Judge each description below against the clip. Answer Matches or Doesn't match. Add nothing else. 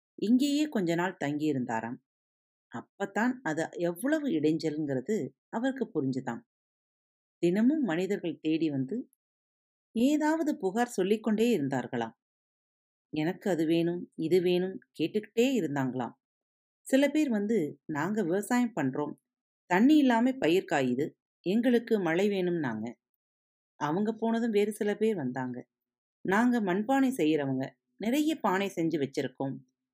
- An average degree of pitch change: Doesn't match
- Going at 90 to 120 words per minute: Matches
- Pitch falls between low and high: Matches